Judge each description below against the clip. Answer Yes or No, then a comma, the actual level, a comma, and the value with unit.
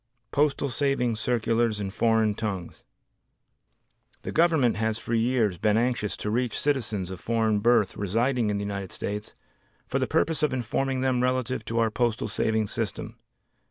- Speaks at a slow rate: No, average, 160 wpm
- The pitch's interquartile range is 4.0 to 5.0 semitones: No, average, 3.2 semitones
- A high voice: No, low, 115 Hz